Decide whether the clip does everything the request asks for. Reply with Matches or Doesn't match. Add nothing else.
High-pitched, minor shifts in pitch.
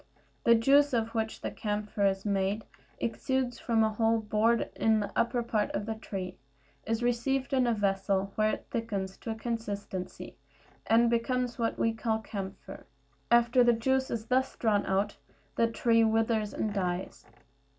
Matches